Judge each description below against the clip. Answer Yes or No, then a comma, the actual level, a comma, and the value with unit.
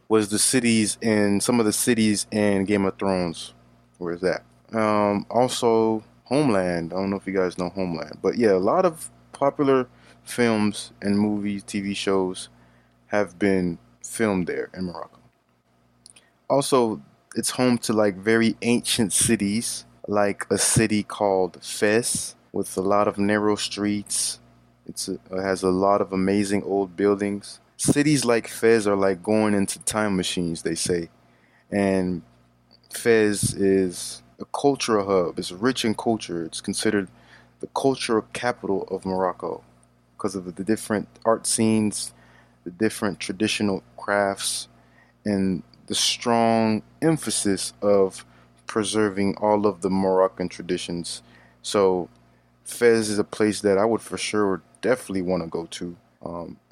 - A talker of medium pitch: No, low, 100 Hz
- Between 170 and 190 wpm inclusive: No, average, 145 wpm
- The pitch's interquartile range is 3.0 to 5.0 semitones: Yes, average, 3.4 semitones